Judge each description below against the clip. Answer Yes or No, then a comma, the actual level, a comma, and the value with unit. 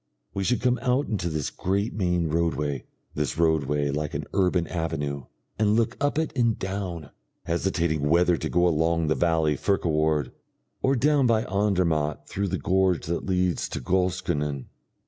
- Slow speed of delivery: No, average, 165 wpm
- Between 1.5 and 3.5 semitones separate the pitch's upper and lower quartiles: No, average, 4.2 semitones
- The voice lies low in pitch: Yes, very low, 85 Hz